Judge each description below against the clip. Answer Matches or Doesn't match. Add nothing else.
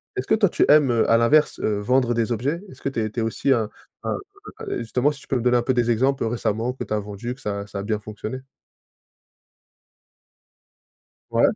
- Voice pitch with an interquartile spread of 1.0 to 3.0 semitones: Doesn't match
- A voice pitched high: Doesn't match